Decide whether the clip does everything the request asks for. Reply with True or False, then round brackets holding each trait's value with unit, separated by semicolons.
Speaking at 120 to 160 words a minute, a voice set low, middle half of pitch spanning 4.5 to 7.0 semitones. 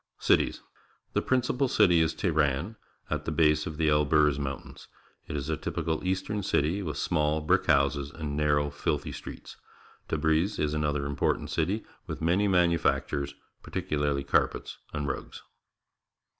False (150 wpm; 75 Hz; 2.9 semitones)